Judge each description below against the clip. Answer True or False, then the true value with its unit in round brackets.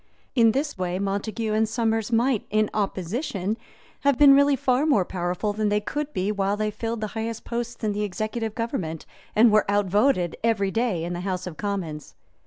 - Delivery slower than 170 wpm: False (190 wpm)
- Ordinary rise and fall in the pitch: True (3.1 semitones)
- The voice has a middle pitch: False (215 Hz)